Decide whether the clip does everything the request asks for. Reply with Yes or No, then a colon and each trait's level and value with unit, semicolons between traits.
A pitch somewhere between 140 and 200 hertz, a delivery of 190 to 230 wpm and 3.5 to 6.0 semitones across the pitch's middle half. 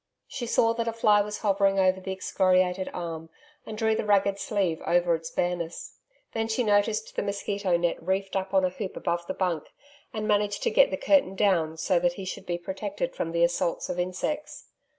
No: high, 190 Hz; fast, 205 wpm; average, 3.0 semitones